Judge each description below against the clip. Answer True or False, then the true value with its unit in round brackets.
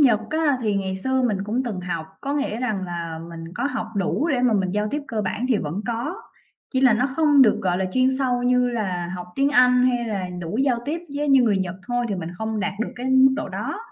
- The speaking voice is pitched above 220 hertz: True (235 Hz)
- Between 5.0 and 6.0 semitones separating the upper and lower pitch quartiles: True (5.4 semitones)